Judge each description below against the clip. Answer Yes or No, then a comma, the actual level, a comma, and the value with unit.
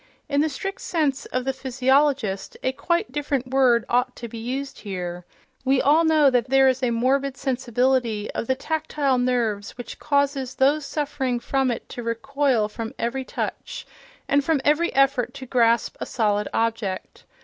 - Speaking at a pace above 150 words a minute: Yes, average, 170 wpm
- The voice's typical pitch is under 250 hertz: No, very high, 260 Hz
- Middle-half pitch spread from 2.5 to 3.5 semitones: Yes, average, 2.9 semitones